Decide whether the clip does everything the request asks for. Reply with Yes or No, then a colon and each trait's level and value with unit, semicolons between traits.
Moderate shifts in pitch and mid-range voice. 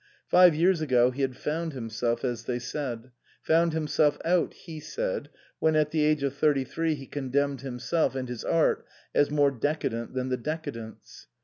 Yes: average, 3.9 semitones; medium, 145 Hz